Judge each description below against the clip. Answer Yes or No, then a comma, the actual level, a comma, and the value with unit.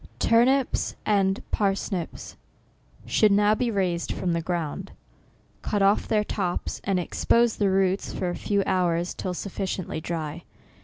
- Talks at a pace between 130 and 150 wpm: Yes, average, 140 wpm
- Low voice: No, high, 195 Hz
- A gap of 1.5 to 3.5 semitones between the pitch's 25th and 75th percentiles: Yes, average, 2.8 semitones